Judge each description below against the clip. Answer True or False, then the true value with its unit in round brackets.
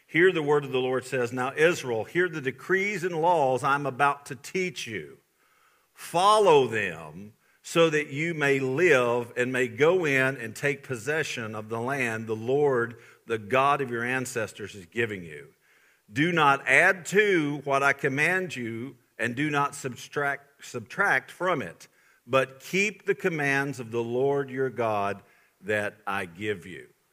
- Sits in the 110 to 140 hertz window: True (135 Hz)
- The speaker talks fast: False (165 wpm)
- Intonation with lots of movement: False (4.1 semitones)